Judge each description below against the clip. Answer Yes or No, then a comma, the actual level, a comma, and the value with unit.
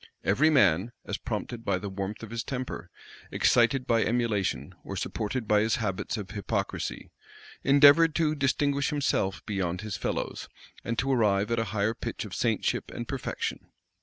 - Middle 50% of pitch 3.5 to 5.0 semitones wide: Yes, average, 4.7 semitones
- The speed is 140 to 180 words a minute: Yes, average, 165 wpm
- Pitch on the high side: No, low, 115 Hz